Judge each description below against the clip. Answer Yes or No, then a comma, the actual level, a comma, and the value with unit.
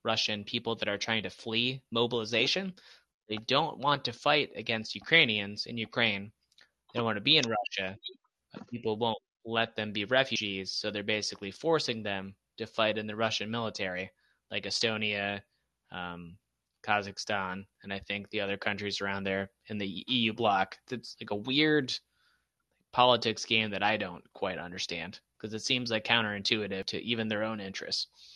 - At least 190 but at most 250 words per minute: No, average, 165 wpm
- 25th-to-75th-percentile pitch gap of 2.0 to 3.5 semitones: Yes, narrow, 2.6 semitones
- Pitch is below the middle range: Yes, low, 110 Hz